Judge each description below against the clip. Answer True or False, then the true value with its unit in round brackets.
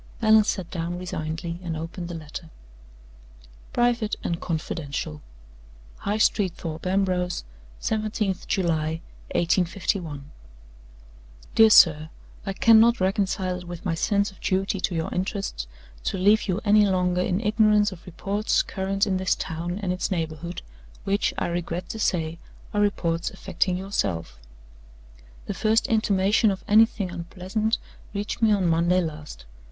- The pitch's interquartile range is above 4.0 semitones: False (3.4 semitones)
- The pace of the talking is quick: False (135 wpm)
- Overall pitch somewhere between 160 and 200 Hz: True (185 Hz)